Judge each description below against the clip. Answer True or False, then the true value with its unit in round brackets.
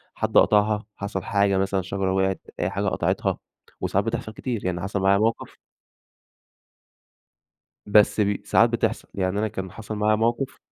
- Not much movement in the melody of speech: True (2.0 semitones)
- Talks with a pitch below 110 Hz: True (100 Hz)